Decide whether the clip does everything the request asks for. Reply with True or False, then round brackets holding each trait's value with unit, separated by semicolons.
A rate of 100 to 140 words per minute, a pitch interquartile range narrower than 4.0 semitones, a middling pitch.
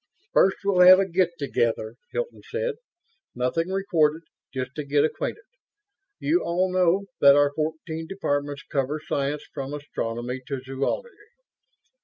False (135 wpm; 5.0 semitones; 155 Hz)